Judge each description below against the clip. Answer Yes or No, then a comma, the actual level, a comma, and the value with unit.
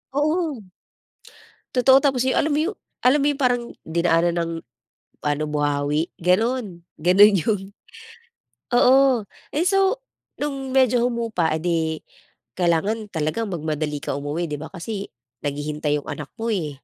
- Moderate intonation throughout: No, wide, 8.7 semitones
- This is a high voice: Yes, high, 195 Hz